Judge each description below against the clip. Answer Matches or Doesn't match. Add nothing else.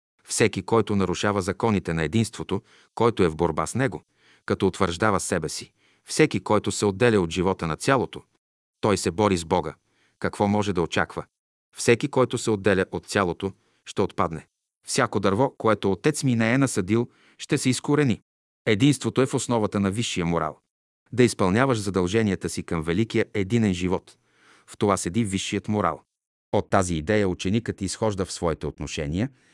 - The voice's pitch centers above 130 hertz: Doesn't match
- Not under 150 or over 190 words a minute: Matches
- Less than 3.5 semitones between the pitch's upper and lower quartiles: Doesn't match